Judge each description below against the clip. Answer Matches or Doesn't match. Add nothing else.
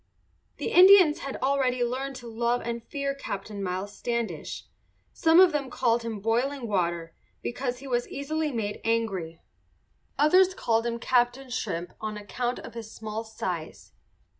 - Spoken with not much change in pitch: Doesn't match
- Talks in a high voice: Matches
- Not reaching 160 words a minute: Matches